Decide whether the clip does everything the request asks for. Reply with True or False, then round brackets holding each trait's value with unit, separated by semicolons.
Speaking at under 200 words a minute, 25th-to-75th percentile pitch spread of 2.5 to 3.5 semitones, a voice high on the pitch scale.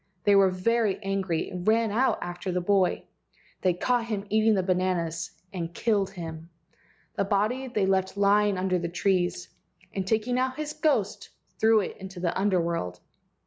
True (170 wpm; 3.2 semitones; 195 Hz)